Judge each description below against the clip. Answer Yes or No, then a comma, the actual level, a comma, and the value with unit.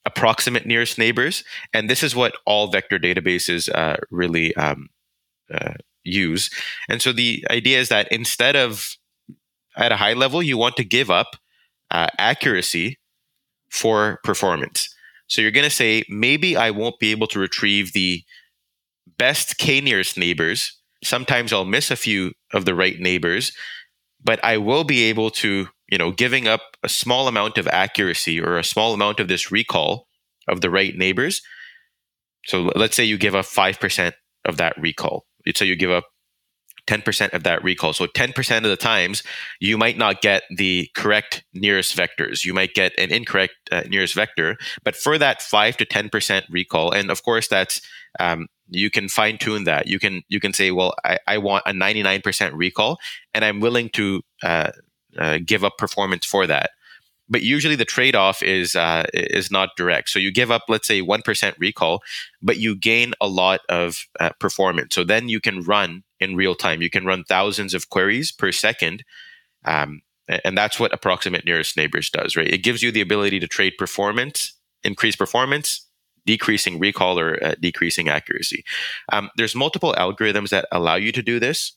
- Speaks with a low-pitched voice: Yes, low, 100 Hz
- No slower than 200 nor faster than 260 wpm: No, average, 185 wpm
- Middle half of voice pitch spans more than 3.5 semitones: Yes, average, 3.9 semitones